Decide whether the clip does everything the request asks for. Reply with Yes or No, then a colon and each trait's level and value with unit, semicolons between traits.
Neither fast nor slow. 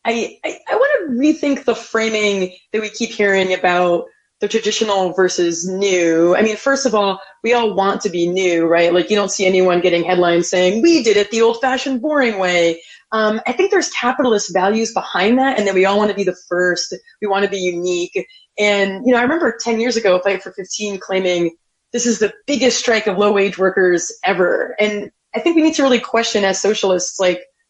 No: fast, 215 wpm